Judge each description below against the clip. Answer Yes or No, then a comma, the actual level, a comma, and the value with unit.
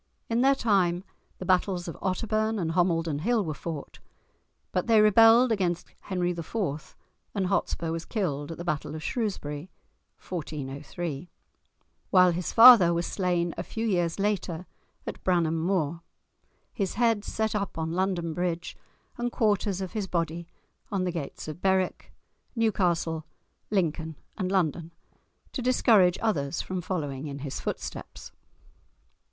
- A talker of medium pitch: Yes, medium, 180 Hz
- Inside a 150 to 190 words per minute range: No, average, 140 wpm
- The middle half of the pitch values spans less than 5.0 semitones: Yes, average, 3.7 semitones